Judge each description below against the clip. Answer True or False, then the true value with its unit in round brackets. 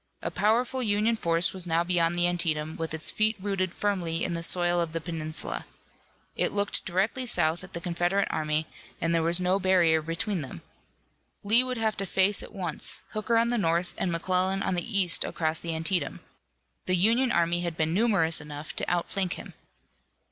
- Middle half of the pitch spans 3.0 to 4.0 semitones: True (3.4 semitones)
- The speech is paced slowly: False (185 wpm)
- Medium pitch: True (175 Hz)